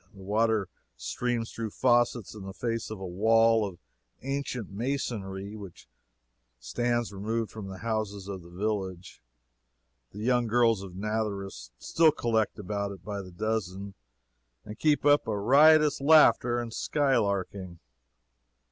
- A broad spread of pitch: No, average, 3.4 semitones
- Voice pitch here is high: No, low, 110 Hz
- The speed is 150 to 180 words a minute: No, average, 140 wpm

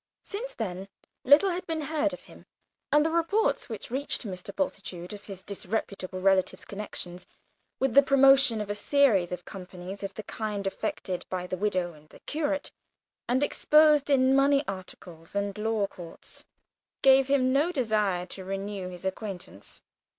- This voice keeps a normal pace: Yes, average, 160 wpm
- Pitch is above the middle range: Yes, high, 210 Hz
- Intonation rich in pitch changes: Yes, wide, 6.8 semitones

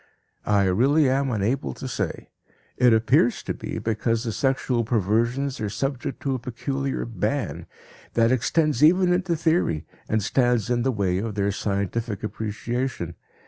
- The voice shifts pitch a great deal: No, average, 4.2 semitones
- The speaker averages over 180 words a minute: No, average, 150 wpm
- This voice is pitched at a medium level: No, low, 120 Hz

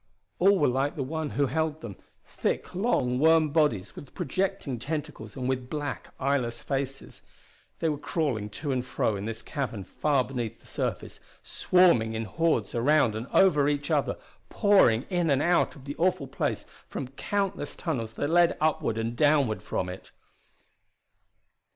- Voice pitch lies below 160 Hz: Yes, medium, 140 Hz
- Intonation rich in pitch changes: No, average, 4.9 semitones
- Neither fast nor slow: Yes, average, 165 wpm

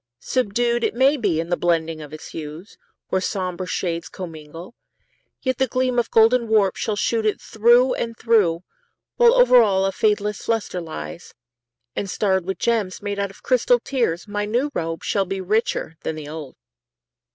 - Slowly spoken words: No, average, 175 wpm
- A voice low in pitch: No, high, 205 Hz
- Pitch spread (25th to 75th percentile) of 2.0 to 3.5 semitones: No, average, 5.2 semitones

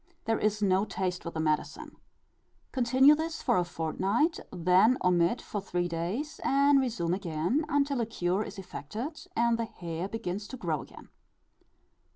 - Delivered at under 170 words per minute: Yes, average, 160 wpm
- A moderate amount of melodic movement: No, wide, 6.3 semitones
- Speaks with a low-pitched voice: No, high, 200 Hz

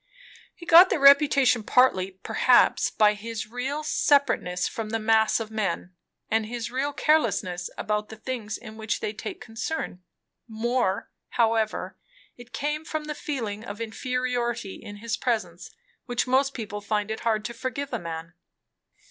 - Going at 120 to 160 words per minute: Yes, average, 155 wpm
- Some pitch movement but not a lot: Yes, average, 3.5 semitones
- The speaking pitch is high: Yes, high, 225 Hz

